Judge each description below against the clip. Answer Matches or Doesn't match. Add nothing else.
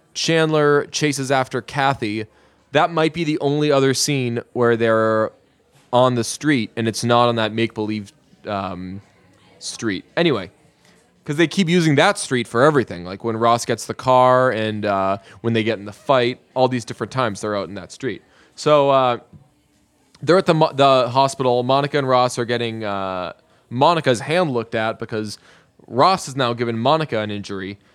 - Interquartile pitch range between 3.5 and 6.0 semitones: Matches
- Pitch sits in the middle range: Doesn't match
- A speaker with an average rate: Matches